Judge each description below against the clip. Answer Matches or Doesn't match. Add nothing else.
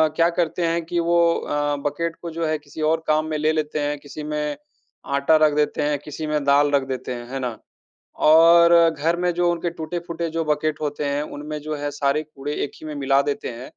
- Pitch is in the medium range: Matches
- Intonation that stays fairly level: Matches